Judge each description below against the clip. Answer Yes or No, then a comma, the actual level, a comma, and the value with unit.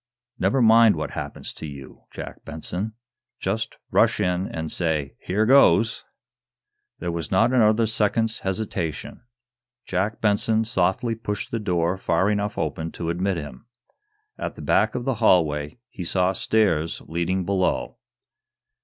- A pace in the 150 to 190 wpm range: No, average, 140 wpm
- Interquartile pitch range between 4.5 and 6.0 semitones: Yes, average, 4.8 semitones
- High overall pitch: No, very low, 95 Hz